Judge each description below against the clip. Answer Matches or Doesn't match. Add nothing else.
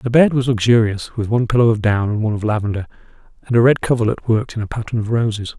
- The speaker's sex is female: Doesn't match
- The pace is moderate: Doesn't match